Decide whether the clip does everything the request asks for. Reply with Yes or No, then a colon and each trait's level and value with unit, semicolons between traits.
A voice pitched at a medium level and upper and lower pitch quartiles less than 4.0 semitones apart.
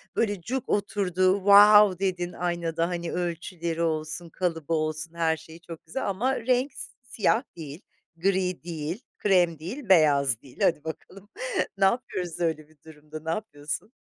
Yes: medium, 175 Hz; average, 3.6 semitones